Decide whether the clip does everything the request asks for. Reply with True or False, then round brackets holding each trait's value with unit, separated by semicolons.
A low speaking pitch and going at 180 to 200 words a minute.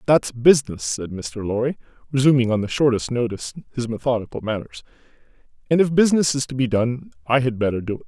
True (125 Hz; 185 wpm)